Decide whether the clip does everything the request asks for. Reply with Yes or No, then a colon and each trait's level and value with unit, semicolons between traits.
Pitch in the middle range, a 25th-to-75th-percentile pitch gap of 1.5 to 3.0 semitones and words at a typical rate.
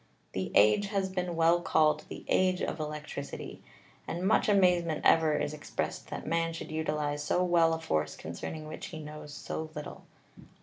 Yes: medium, 160 Hz; narrow, 2.4 semitones; average, 170 wpm